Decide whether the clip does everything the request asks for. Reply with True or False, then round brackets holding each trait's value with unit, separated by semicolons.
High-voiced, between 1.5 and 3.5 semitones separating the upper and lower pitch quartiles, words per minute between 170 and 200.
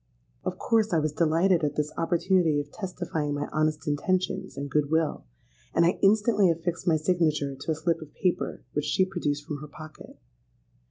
False (160 Hz; 3.2 semitones; 180 wpm)